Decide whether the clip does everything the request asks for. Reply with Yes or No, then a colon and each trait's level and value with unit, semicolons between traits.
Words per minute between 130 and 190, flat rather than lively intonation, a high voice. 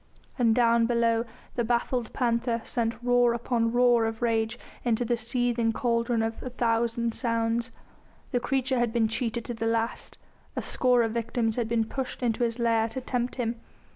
Yes: average, 175 wpm; narrow, 1.2 semitones; high, 235 Hz